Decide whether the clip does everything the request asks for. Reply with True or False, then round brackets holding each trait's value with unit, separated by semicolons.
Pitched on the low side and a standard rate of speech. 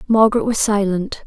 False (210 Hz; 145 wpm)